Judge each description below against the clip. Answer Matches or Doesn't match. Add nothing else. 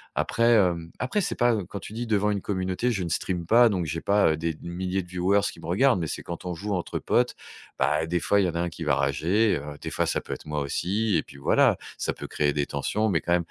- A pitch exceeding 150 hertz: Doesn't match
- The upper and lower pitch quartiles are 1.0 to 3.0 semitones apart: Doesn't match